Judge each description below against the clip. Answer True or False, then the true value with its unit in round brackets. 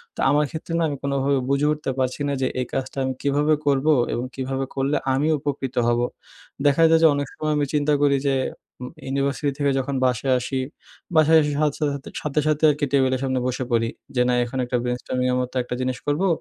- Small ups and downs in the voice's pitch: True (2.1 semitones)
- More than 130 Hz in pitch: True (140 Hz)